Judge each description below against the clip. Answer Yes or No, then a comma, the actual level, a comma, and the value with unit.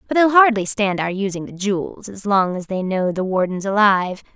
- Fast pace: Yes, fast, 220 wpm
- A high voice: Yes, high, 200 Hz